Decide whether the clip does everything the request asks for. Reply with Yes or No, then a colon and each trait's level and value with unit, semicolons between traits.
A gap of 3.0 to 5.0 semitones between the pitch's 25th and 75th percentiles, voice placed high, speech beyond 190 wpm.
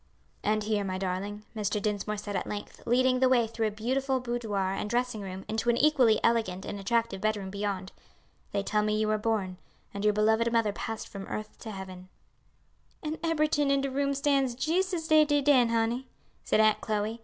Yes: average, 3.8 semitones; high, 220 Hz; average, 200 wpm